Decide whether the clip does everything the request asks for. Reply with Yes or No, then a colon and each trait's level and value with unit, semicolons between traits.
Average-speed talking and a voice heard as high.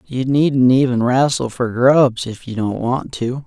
No: average, 190 wpm; low, 125 Hz